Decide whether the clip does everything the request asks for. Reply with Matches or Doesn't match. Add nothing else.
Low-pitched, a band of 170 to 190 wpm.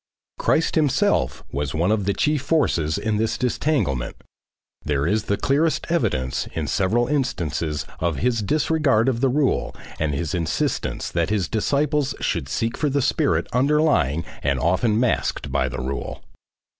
Doesn't match